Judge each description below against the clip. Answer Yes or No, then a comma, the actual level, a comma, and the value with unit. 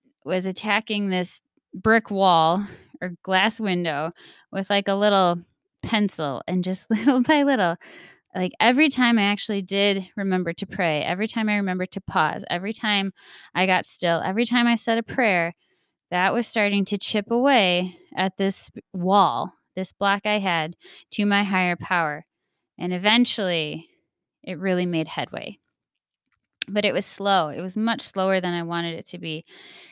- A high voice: Yes, high, 195 Hz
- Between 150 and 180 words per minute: Yes, average, 160 wpm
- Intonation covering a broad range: No, average, 2.9 semitones